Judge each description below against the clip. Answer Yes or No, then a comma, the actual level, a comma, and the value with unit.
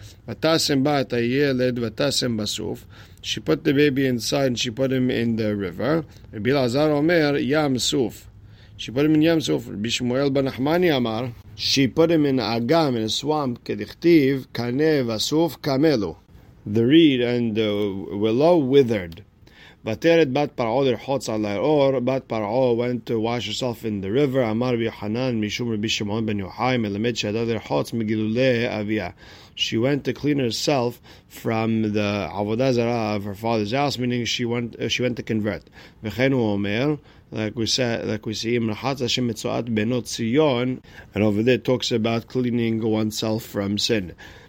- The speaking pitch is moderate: No, low, 120 Hz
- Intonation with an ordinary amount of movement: Yes, average, 3.7 semitones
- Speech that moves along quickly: No, average, 160 wpm